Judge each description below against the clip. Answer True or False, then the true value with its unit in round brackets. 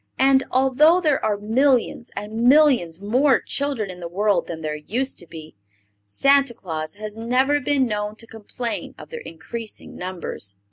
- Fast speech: False (160 wpm)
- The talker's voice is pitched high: True (225 Hz)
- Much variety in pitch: True (6.4 semitones)